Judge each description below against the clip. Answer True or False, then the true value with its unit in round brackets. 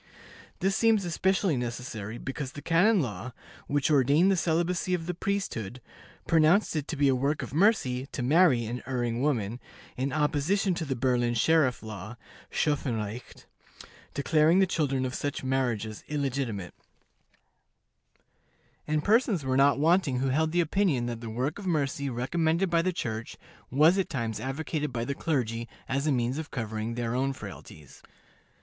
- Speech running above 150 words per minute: True (160 wpm)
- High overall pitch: False (140 Hz)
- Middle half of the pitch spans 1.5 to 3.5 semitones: False (5.2 semitones)